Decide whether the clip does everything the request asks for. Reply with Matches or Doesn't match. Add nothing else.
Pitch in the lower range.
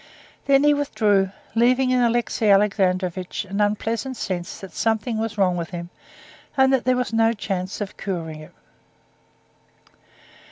Doesn't match